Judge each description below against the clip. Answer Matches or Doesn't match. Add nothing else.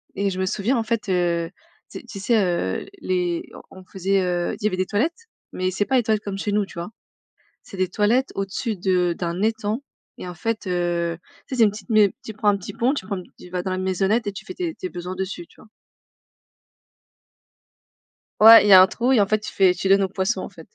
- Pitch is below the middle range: Doesn't match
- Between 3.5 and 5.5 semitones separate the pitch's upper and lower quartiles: Doesn't match